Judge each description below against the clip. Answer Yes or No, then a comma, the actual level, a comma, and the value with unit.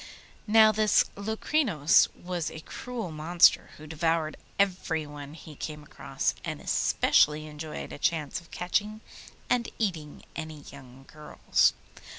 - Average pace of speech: No, slow, 125 wpm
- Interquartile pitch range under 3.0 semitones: No, average, 4.9 semitones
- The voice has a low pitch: No, medium, 160 Hz